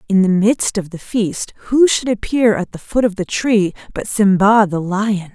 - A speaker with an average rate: No, fast, 215 wpm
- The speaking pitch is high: Yes, high, 205 Hz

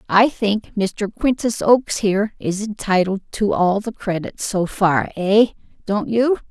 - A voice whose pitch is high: Yes, high, 205 Hz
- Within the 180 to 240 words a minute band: No, average, 140 wpm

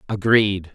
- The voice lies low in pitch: Yes, low, 100 Hz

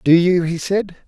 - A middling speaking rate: No, fast, 225 wpm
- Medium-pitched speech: Yes, medium, 175 Hz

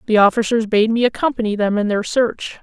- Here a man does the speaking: No, female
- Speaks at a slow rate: No, fast, 205 wpm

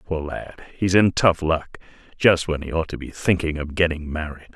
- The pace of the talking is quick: No, average, 195 wpm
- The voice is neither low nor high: No, very low, 80 Hz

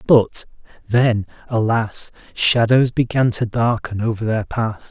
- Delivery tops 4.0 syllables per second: No, 3.8 syllables/s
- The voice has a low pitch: Yes, low, 115 Hz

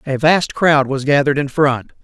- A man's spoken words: Yes, male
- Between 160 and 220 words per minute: Yes, fast, 205 wpm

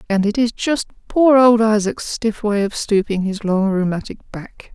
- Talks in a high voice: Yes, high, 215 Hz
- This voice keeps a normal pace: Yes, average, 190 wpm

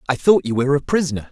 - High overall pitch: No, low, 135 Hz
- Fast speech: Yes, fast, 275 wpm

